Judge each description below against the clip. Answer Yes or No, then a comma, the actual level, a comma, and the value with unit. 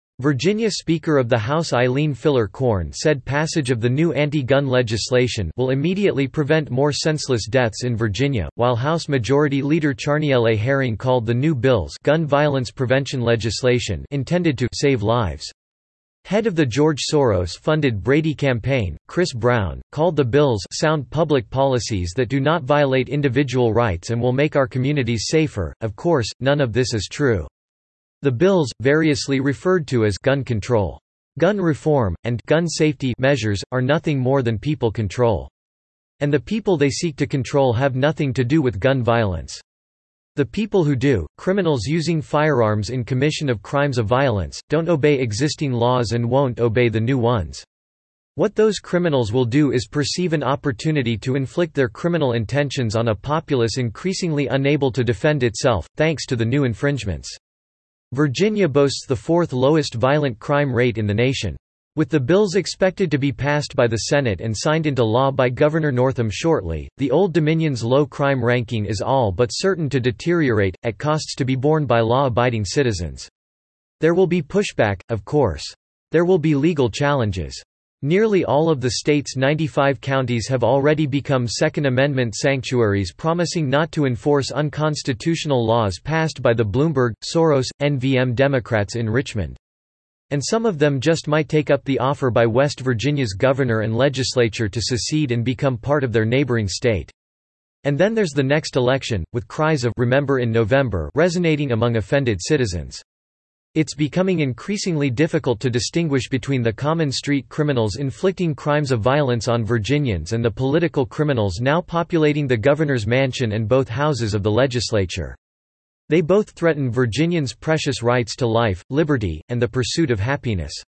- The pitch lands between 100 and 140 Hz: Yes, low, 135 Hz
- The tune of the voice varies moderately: Yes, average, 4.3 semitones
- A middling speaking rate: Yes, average, 165 wpm